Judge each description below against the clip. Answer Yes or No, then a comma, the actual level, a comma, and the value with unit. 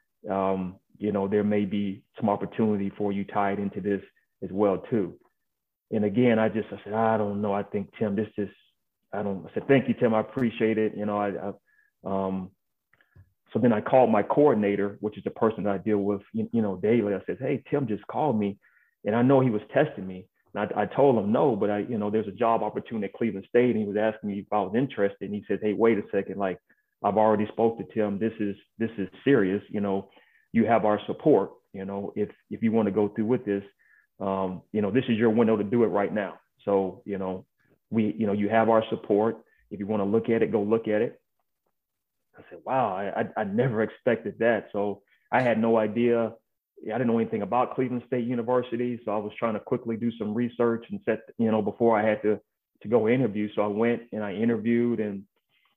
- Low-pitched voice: Yes, low, 105 Hz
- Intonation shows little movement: Yes, narrow, 2.2 semitones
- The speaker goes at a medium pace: No, fast, 235 wpm